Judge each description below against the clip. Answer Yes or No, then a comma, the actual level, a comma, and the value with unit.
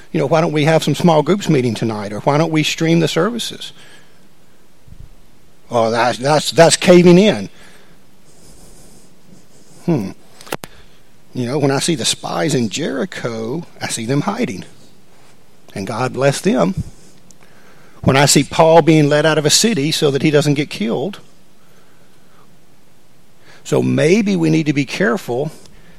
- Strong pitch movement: No, average, 4.0 semitones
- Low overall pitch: No, medium, 155 Hz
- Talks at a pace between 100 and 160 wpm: Yes, average, 150 wpm